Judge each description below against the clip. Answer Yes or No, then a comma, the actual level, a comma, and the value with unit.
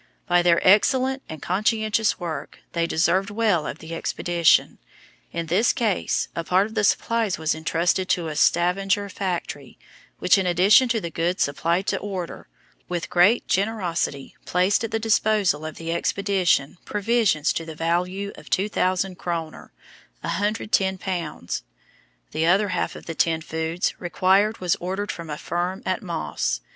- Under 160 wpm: Yes, average, 150 wpm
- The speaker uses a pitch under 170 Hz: No, medium, 180 Hz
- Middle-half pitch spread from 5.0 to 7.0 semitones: No, average, 3.4 semitones